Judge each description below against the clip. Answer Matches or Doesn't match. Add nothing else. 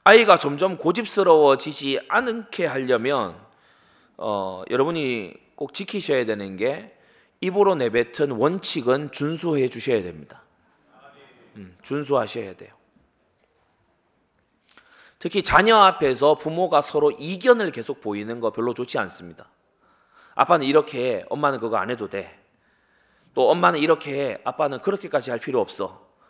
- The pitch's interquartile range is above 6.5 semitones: Matches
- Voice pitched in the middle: Matches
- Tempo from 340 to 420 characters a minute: Doesn't match